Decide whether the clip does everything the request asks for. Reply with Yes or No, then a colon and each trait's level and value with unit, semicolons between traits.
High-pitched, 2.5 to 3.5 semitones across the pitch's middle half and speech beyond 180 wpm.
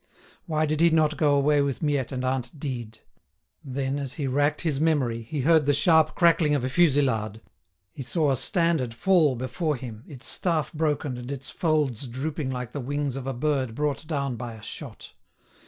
No: medium, 140 Hz; average, 3.2 semitones; average, 190 wpm